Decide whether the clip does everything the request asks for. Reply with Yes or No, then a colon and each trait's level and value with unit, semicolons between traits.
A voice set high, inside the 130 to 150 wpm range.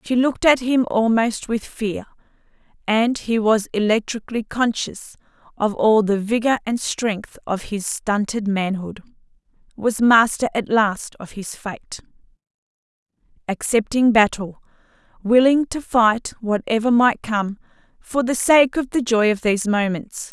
Yes: high, 225 Hz; slow, 135 wpm